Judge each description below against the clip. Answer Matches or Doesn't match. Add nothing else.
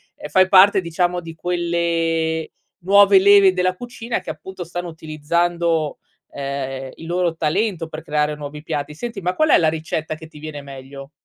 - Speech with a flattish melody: Doesn't match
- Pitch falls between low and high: Matches